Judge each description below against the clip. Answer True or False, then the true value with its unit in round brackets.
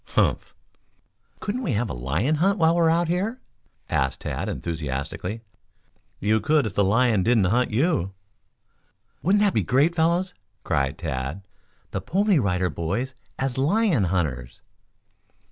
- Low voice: True (120 Hz)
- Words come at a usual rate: True (145 wpm)